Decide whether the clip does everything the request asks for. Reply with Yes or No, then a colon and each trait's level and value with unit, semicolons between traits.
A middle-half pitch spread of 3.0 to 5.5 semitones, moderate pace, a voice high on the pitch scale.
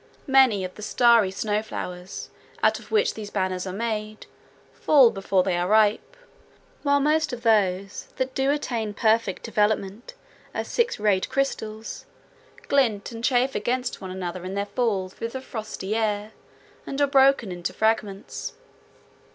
Yes: average, 4.5 semitones; average, 150 wpm; high, 215 Hz